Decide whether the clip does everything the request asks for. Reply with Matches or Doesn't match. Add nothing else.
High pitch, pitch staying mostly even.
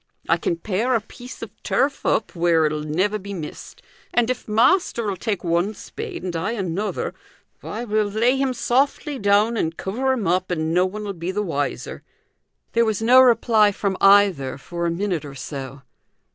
Doesn't match